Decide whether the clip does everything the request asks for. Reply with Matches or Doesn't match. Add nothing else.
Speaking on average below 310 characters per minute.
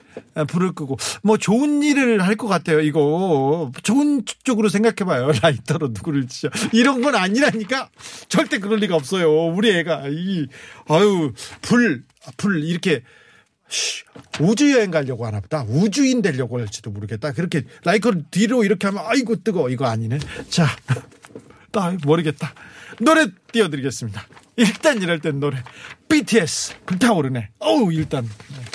Doesn't match